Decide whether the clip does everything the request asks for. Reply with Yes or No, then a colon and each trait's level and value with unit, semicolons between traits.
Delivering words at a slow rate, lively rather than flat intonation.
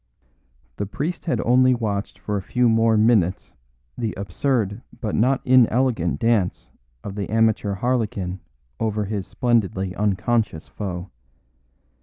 No: slow, 125 wpm; average, 3.4 semitones